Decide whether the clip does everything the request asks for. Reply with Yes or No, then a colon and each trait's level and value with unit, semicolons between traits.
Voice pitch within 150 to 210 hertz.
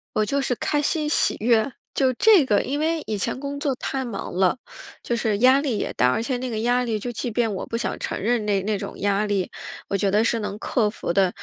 No: high, 230 Hz